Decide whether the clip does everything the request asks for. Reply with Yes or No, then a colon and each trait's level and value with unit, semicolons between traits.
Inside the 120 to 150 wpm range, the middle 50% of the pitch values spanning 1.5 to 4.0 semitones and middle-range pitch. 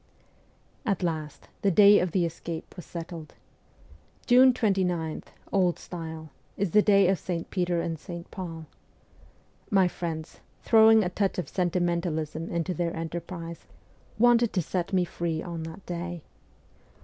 Yes: average, 140 wpm; average, 2.7 semitones; medium, 175 Hz